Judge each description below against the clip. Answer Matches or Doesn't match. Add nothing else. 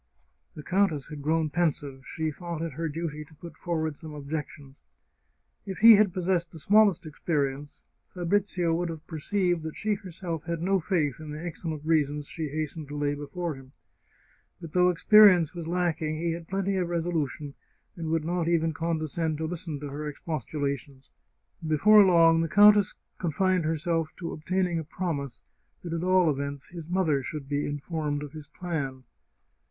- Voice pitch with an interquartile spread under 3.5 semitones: Matches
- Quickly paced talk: Doesn't match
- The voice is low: Doesn't match